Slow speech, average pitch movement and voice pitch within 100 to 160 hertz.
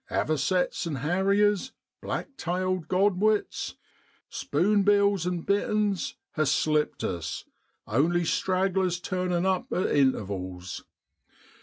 No: slow, 105 wpm; average, 4.4 semitones; medium, 180 Hz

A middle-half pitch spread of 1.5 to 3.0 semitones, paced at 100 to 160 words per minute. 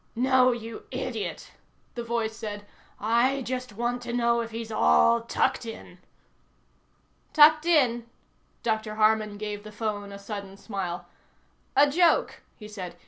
Yes: narrow, 2.6 semitones; average, 140 wpm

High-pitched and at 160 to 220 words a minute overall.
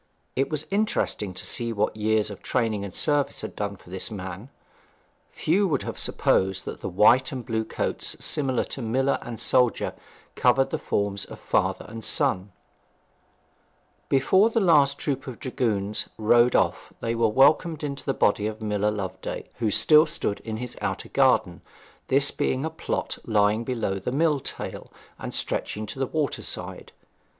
No: low, 115 Hz; average, 170 wpm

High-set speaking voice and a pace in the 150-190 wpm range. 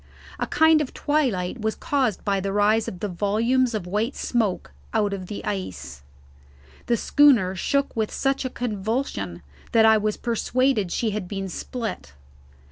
Yes: high, 215 Hz; average, 160 wpm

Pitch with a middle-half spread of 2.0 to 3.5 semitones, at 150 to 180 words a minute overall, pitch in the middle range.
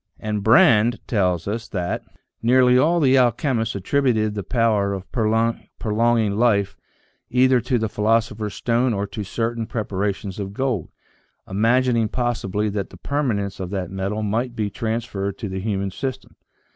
No: average, 3.1 semitones; average, 160 wpm; low, 110 Hz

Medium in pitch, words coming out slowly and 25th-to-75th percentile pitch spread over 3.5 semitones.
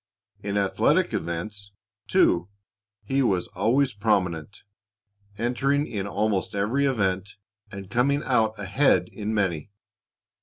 No: low, 105 Hz; slow, 110 wpm; average, 4.2 semitones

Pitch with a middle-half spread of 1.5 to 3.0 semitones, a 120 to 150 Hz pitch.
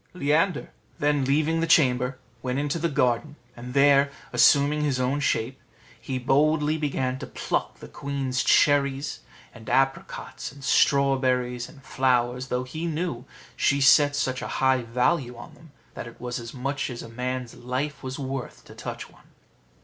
Yes: narrow, 2.6 semitones; low, 135 Hz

